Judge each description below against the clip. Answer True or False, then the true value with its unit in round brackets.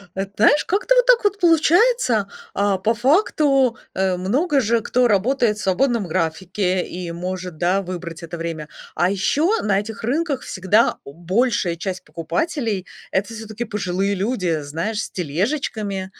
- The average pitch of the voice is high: True (205 Hz)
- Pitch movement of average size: False (5.9 semitones)